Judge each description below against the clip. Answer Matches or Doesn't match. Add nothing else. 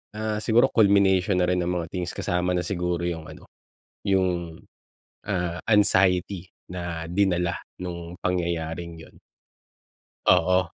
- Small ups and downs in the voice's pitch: Matches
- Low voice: Matches